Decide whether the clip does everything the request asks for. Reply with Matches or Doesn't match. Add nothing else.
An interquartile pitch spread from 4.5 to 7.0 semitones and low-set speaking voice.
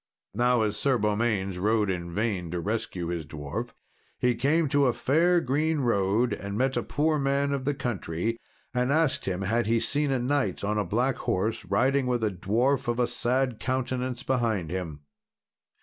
Matches